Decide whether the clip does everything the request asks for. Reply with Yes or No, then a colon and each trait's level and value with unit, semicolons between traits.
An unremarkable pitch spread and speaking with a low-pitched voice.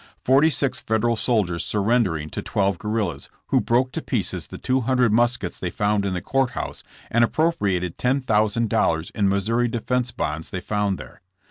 Yes: average, 4.3 semitones; low, 110 Hz